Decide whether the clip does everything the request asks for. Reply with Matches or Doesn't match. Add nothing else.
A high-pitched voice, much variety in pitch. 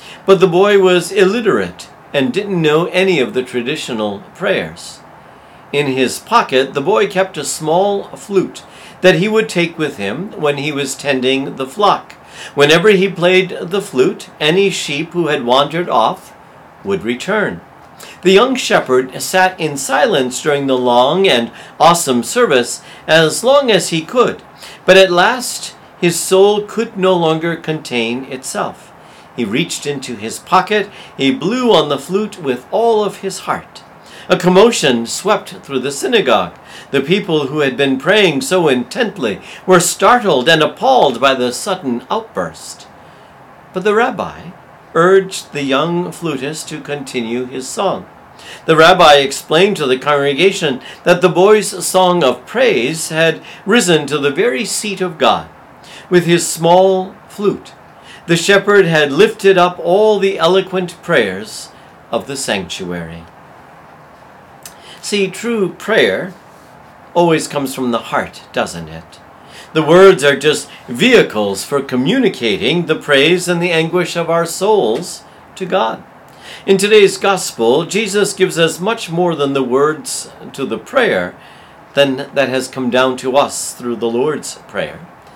Doesn't match